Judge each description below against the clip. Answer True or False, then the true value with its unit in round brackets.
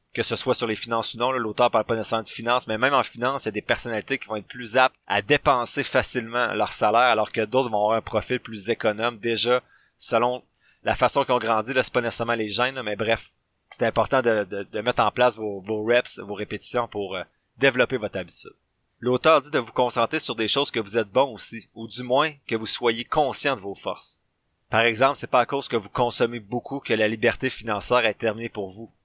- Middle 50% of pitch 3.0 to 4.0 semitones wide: False (2.4 semitones)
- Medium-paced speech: False (240 wpm)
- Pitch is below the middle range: True (115 Hz)